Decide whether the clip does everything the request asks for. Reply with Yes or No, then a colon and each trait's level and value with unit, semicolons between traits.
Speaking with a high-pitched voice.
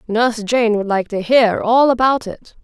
Yes: high, 225 Hz